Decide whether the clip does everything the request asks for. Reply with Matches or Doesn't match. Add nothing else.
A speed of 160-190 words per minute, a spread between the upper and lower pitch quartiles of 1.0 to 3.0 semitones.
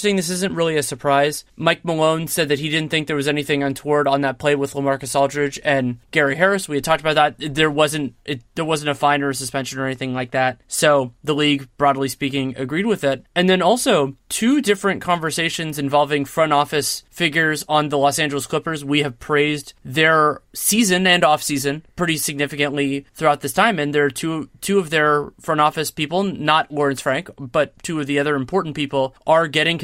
Doesn't match